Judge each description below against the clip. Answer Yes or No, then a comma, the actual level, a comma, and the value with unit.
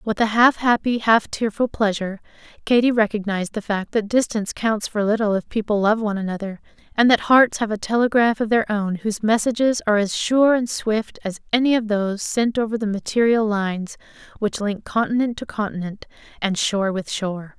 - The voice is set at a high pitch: Yes, high, 215 Hz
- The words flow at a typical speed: Yes, average, 190 wpm